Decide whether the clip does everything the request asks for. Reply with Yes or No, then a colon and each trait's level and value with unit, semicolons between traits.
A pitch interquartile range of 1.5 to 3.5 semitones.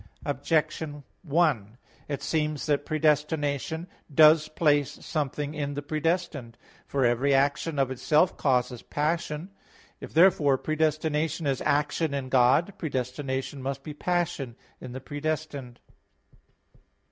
Yes: narrow, 2.5 semitones